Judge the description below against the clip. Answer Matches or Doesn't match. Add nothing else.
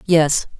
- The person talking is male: Doesn't match